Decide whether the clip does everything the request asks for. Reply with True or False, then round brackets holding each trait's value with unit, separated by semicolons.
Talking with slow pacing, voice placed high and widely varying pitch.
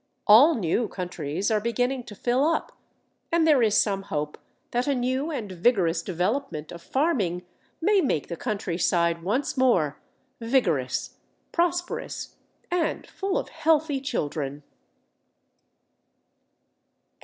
True (120 wpm; 230 Hz; 8.3 semitones)